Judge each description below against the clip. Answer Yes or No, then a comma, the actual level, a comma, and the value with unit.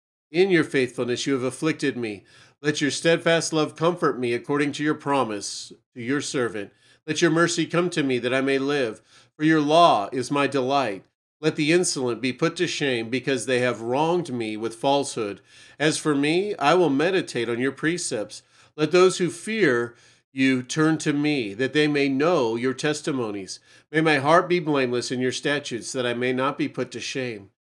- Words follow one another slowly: No, average, 195 wpm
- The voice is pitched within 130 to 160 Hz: Yes, medium, 140 Hz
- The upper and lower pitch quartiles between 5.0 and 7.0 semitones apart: No, average, 3.9 semitones